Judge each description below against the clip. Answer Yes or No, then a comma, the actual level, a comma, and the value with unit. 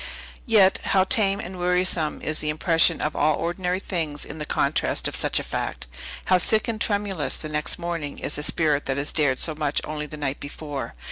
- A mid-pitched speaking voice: Yes, medium, 160 Hz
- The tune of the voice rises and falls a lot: No, average, 3.8 semitones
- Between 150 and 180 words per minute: No, fast, 205 wpm